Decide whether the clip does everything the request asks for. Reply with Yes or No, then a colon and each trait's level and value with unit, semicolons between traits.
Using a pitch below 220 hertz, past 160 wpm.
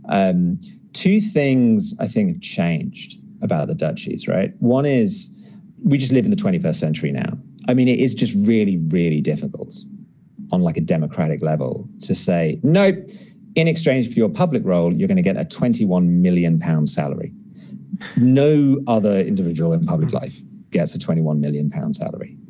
Yes: medium, 140 Hz; average, 175 wpm